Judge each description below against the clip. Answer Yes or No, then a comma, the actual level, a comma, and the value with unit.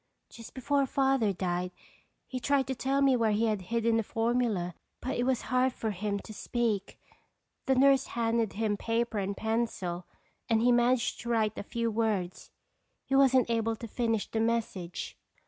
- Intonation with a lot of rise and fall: No, average, 2.7 semitones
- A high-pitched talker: Yes, high, 230 Hz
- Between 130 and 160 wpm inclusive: No, average, 170 wpm